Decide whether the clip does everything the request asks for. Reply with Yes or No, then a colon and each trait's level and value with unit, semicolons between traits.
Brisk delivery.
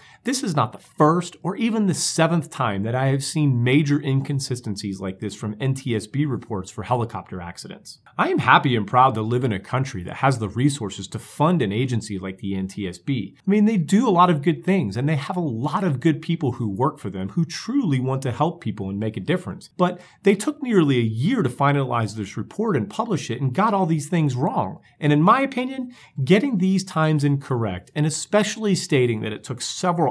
Yes: fast, 220 wpm